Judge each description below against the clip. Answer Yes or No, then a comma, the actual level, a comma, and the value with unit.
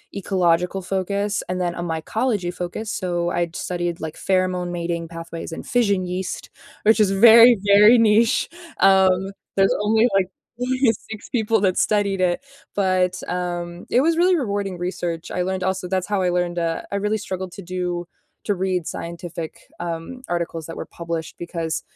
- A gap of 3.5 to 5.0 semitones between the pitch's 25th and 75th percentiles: No, average, 2.8 semitones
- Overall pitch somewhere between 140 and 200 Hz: Yes, medium, 185 Hz